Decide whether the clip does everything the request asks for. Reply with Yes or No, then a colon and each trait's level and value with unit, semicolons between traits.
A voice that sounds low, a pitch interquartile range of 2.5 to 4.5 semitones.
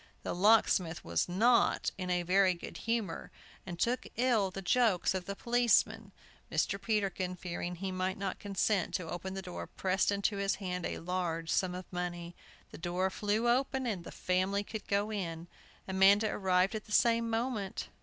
No: high, 190 Hz; average, 2.8 semitones